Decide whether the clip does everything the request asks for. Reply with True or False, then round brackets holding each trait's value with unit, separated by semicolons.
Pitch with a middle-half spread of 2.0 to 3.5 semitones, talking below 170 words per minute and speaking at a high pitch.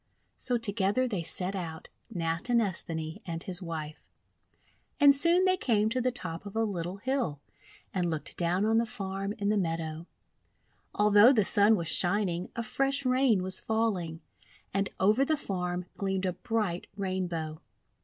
False (4.7 semitones; 155 wpm; 195 Hz)